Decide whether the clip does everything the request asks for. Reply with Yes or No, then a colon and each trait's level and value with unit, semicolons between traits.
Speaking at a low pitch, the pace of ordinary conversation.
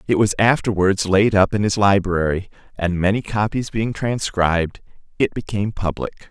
Yes: low, 100 Hz; average, 150 wpm